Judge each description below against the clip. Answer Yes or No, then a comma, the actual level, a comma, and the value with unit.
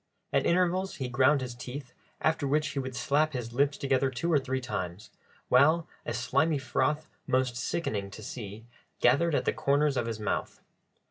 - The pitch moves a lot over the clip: No, average, 3.7 semitones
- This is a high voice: No, low, 130 Hz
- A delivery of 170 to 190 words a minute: Yes, average, 180 wpm